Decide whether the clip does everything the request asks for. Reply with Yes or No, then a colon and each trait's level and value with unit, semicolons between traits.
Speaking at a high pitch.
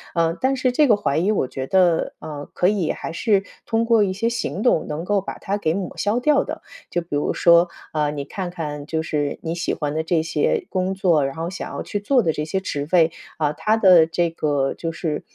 No: medium, 175 Hz